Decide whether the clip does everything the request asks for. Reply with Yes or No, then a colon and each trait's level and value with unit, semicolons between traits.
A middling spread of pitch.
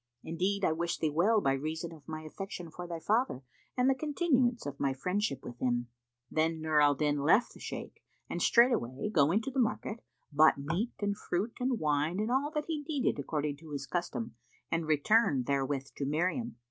No: wide, 7.5 semitones